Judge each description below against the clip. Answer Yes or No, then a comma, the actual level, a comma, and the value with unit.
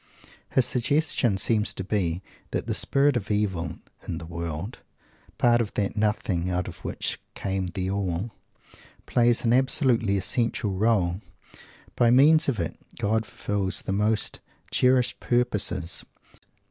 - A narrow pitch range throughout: No, average, 4.3 semitones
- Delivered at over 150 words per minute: No, slow, 135 wpm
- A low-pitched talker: Yes, low, 105 Hz